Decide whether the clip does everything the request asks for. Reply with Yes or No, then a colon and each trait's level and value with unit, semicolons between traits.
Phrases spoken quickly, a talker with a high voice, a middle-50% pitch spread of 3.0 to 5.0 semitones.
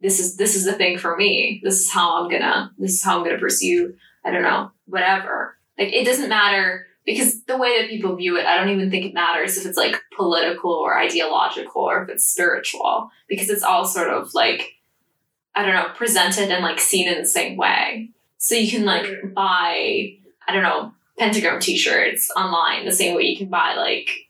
Yes: fast, 210 wpm; high, 195 Hz; average, 3.9 semitones